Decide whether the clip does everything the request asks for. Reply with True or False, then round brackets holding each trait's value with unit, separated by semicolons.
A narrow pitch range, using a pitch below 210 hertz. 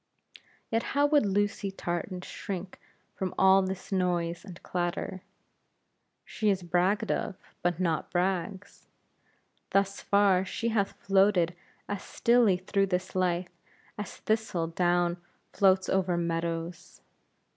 True (2.2 semitones; 185 Hz)